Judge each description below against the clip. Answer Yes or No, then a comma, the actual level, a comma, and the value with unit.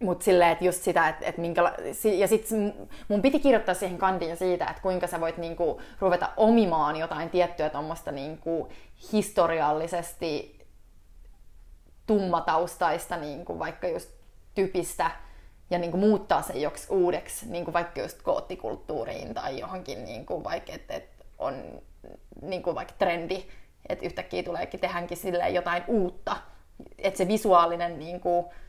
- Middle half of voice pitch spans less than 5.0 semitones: Yes, narrow, 2.5 semitones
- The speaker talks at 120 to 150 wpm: Yes, average, 125 wpm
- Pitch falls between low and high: Yes, medium, 175 Hz